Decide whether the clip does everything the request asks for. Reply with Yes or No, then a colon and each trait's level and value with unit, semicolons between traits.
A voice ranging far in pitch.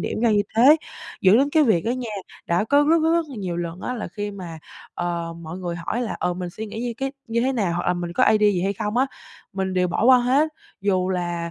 Yes: wide, 5.7 semitones